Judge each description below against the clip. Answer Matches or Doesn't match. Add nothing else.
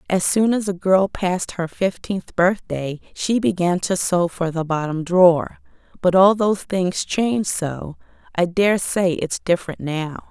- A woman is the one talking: Matches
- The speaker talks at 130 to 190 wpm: Matches